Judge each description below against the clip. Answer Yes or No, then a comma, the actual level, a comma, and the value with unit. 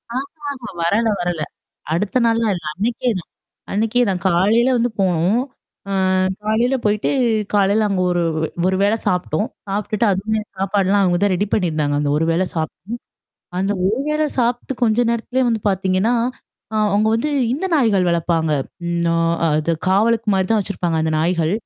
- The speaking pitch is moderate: No, high, 200 Hz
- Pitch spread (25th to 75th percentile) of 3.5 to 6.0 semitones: Yes, average, 4.3 semitones